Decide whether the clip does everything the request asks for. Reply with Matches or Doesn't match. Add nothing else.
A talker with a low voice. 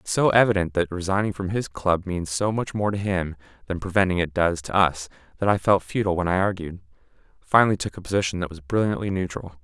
Matches